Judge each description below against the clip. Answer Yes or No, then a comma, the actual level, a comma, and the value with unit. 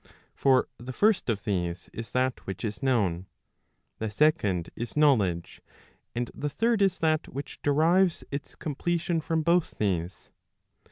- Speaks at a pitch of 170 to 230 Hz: No, low, 130 Hz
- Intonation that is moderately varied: No, wide, 7.7 semitones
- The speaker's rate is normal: Yes, average, 145 wpm